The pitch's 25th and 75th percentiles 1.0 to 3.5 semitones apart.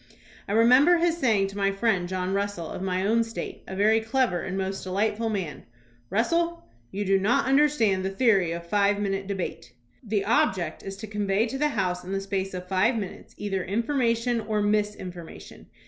Yes: average, 3.1 semitones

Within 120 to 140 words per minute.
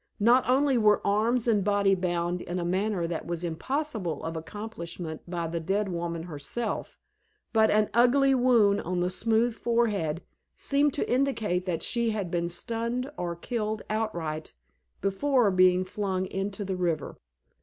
No: average, 155 wpm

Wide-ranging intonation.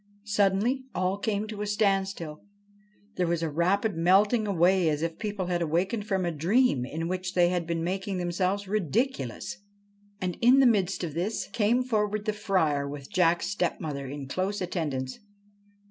No: average, 3.7 semitones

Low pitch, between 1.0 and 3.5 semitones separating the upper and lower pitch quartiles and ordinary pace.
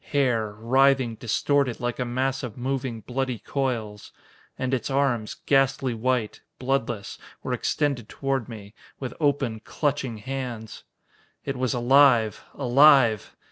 No: low, 125 Hz; average, 2.9 semitones; slow, 125 wpm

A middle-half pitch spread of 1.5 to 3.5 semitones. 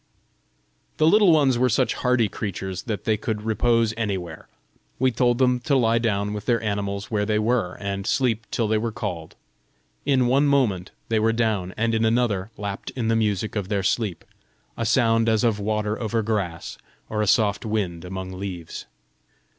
Yes: average, 2.8 semitones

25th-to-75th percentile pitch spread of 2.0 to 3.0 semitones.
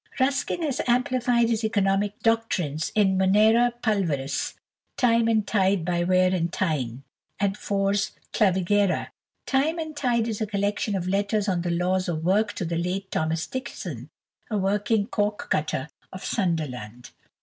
No: average, 3.9 semitones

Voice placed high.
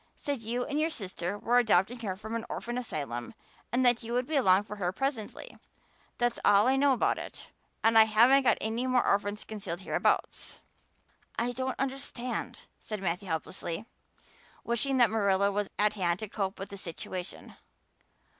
Yes: high, 220 Hz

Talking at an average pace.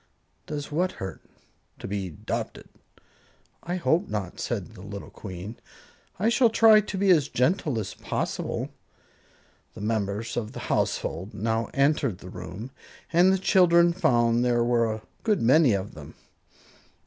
Yes: average, 150 wpm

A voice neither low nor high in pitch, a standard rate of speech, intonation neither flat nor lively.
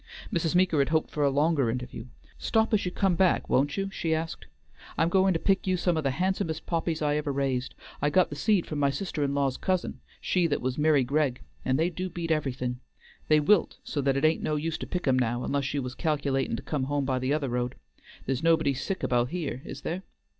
No: medium, 150 Hz; fast, 235 wpm; average, 3.8 semitones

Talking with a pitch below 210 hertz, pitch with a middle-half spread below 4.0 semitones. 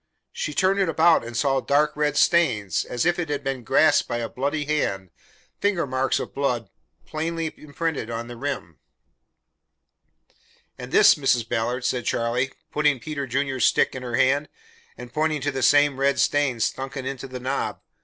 Yes: low, 135 Hz; average, 3.5 semitones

